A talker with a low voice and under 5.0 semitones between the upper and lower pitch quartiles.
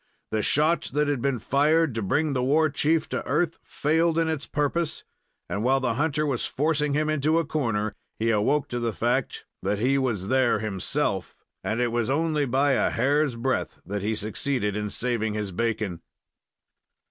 No: low, 130 Hz; average, 5.3 semitones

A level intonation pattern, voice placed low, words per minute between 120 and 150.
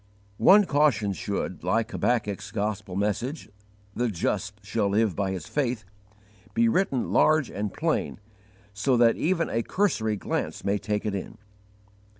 No: average, 5.1 semitones; low, 110 Hz; average, 145 wpm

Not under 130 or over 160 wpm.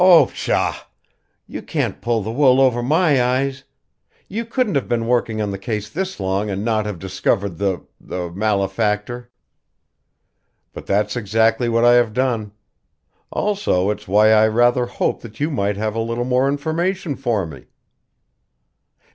Yes: average, 155 wpm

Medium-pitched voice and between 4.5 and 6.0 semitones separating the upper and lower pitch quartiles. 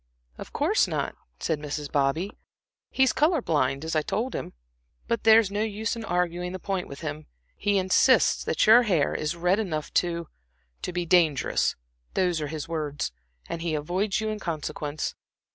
Yes: medium, 175 Hz; average, 5.0 semitones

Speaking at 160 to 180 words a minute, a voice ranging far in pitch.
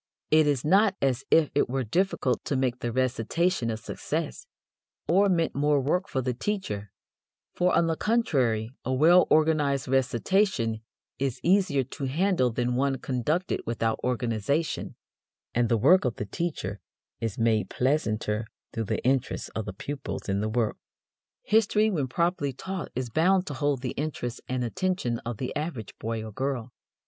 Yes: average, 165 wpm; wide, 6.0 semitones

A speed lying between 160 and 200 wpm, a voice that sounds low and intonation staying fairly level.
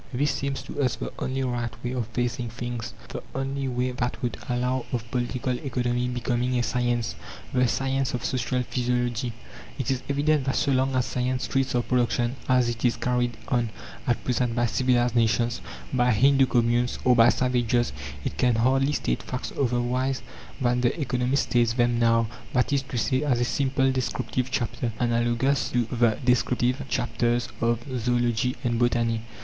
Yes: average, 175 wpm; low, 125 Hz; narrow, 1.3 semitones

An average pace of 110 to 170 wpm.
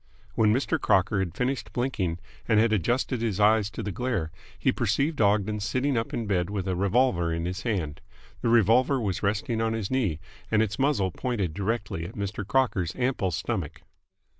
No: average, 185 wpm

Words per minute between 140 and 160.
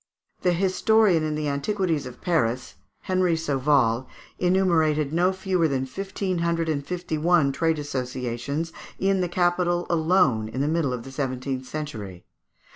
Yes: average, 145 wpm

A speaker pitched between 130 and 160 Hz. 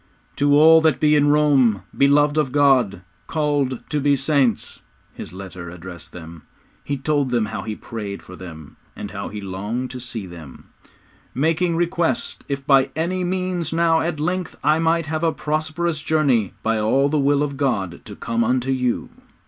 Yes: medium, 140 Hz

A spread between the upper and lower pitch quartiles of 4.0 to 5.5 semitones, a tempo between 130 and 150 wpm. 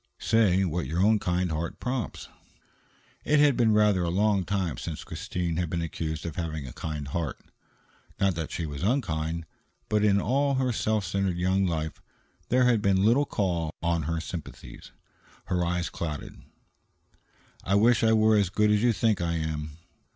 No: average, 4.5 semitones; average, 175 wpm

